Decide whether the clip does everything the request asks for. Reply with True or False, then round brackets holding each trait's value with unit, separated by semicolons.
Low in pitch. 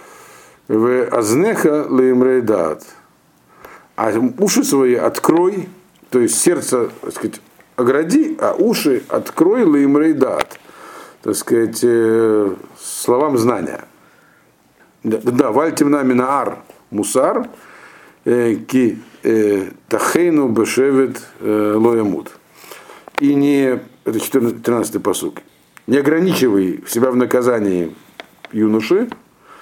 True (130 Hz)